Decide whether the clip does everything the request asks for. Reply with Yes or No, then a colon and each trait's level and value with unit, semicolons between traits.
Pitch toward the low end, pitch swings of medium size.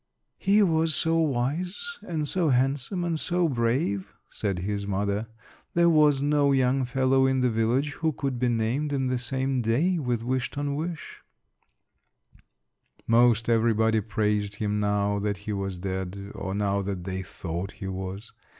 No: low, 120 Hz; wide, 6.0 semitones